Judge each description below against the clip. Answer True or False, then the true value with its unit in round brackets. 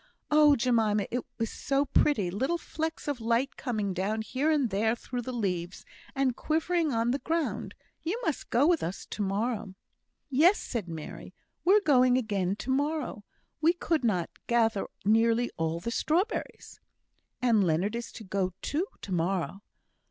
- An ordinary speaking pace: True (160 wpm)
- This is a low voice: False (235 Hz)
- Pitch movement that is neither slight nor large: False (6.3 semitones)